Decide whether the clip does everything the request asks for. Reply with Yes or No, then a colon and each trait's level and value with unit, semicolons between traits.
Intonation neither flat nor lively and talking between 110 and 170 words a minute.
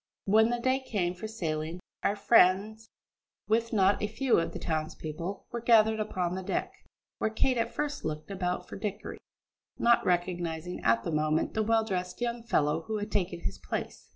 No: average, 4.4 semitones; average, 180 wpm